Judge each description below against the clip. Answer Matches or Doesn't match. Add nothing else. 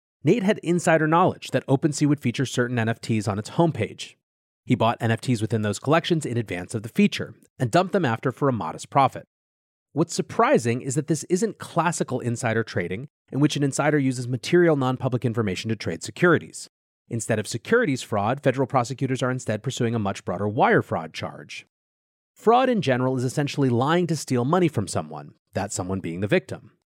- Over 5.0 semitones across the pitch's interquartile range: Matches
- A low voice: Matches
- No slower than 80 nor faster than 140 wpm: Doesn't match